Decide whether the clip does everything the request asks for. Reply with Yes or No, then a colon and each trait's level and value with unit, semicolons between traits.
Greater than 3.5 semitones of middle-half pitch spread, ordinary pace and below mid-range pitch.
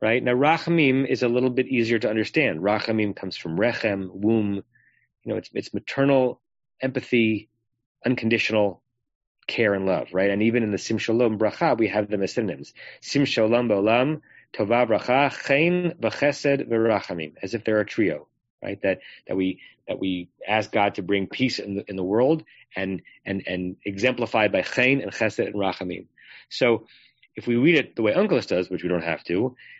Yes: average, 4.1 semitones; average, 180 wpm; low, 110 Hz